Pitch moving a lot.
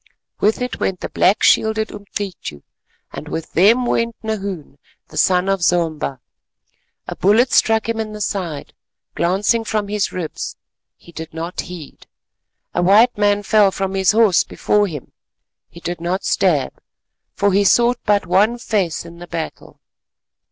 No: average, 3.8 semitones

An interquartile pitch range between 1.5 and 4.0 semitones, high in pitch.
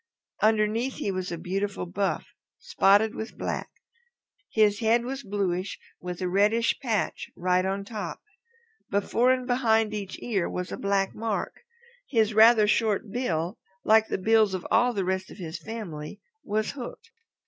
Yes: average, 3.0 semitones; high, 210 Hz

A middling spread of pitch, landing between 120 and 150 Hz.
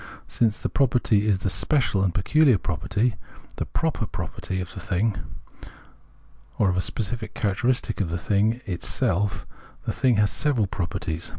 No: average, 4.2 semitones; low, 105 Hz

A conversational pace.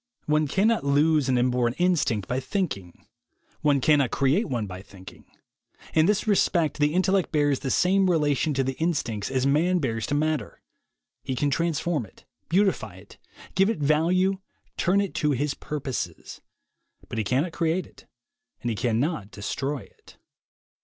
Yes: average, 160 wpm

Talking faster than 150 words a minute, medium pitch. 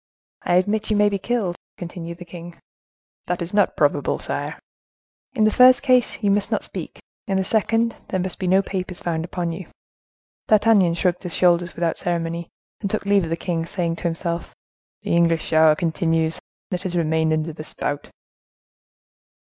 Yes: average, 175 wpm; medium, 175 Hz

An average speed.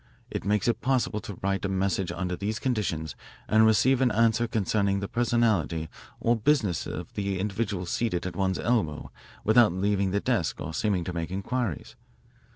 Yes: average, 170 wpm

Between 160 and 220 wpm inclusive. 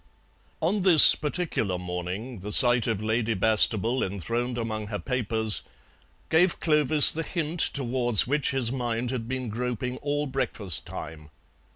No: average, 140 wpm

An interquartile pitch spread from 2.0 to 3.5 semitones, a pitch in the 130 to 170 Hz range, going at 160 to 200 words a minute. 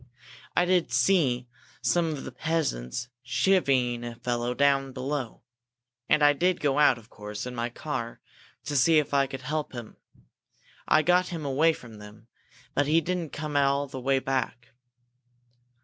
No: average, 4.1 semitones; low, 135 Hz; average, 165 wpm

